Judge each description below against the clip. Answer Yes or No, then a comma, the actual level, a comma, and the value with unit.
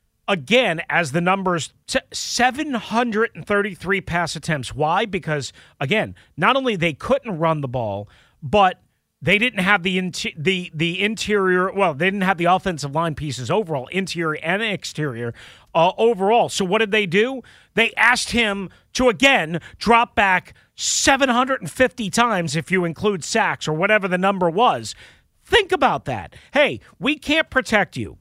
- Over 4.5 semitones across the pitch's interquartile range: Yes, wide, 5.6 semitones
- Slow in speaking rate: No, average, 150 wpm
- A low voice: No, high, 190 Hz